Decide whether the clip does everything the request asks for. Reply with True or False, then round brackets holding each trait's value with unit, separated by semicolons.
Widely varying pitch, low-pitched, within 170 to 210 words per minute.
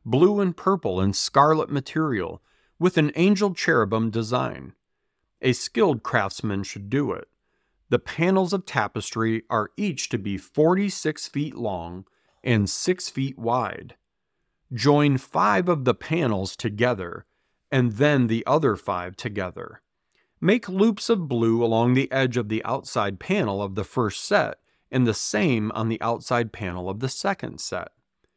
False (5.9 semitones; 125 Hz; 150 wpm)